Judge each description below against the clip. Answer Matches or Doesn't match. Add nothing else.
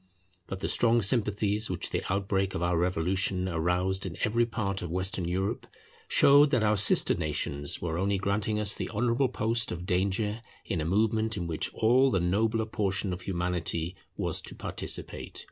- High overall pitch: Doesn't match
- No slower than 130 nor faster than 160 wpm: Doesn't match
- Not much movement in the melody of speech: Doesn't match